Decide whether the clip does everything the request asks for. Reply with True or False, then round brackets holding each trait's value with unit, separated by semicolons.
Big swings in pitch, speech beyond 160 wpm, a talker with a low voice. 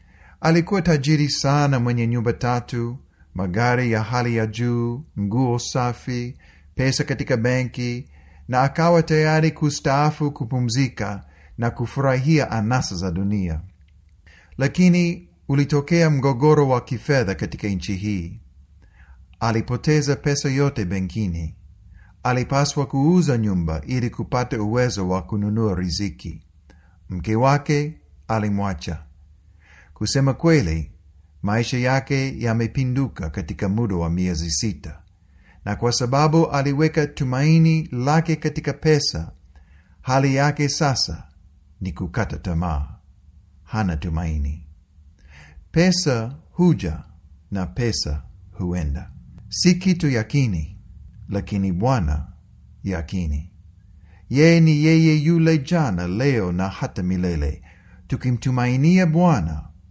False (8.1 semitones; 100 wpm; 110 Hz)